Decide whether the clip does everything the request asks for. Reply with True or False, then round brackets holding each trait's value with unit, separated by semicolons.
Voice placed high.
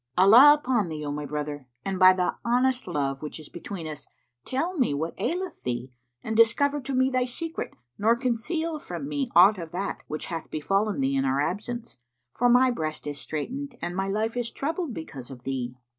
True (200 Hz)